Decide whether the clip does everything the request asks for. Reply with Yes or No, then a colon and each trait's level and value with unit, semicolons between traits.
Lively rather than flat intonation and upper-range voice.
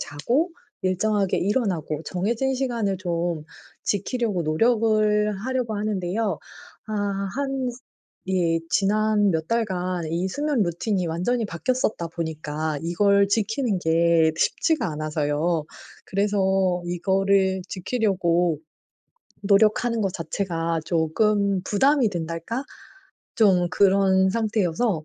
No: average, 4.3 semitones; high, 195 Hz